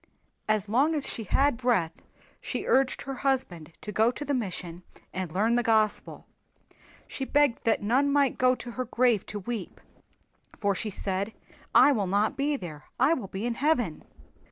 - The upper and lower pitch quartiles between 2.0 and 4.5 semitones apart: No, average, 4.9 semitones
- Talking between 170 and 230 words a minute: Yes, average, 180 wpm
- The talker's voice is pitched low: No, high, 230 Hz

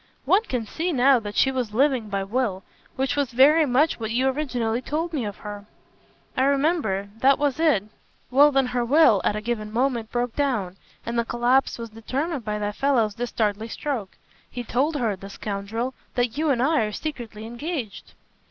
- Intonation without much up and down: No, average, 4.3 semitones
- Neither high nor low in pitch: No, high, 245 Hz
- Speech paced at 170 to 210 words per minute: Yes, average, 190 wpm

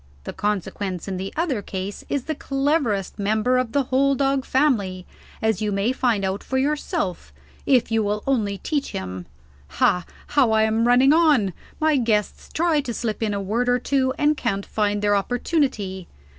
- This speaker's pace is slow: No, average, 180 wpm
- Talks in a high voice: Yes, high, 225 Hz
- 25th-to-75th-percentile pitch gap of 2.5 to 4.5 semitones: No, average, 5.2 semitones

